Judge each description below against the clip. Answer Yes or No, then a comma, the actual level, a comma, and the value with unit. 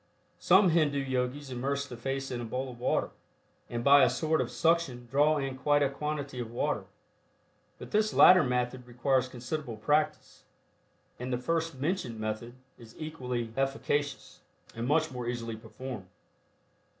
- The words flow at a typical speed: Yes, average, 155 wpm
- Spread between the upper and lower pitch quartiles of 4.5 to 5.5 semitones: No, average, 3.4 semitones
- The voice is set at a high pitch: No, low, 135 Hz